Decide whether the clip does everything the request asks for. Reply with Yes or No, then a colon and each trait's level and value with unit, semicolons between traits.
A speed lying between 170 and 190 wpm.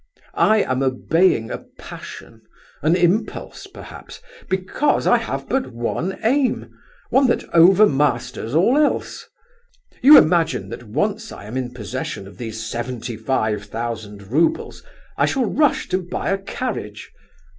No: slow, 135 wpm